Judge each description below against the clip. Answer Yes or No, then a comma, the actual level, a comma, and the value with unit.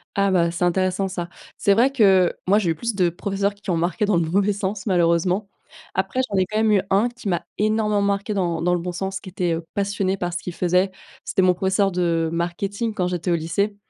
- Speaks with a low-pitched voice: No, high, 190 Hz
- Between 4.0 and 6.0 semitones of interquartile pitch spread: No, narrow, 2.4 semitones